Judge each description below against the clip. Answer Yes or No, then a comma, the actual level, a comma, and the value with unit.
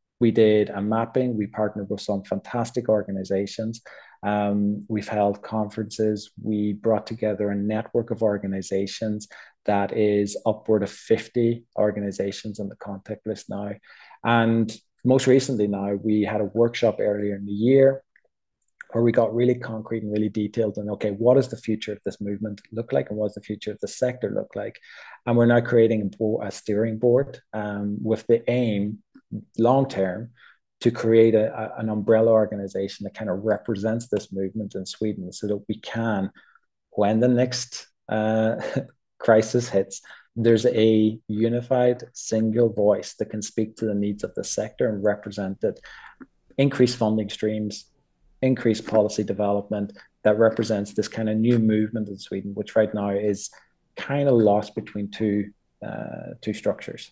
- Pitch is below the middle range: Yes, low, 110 Hz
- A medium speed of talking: Yes, average, 165 wpm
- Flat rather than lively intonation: Yes, narrow, 1.8 semitones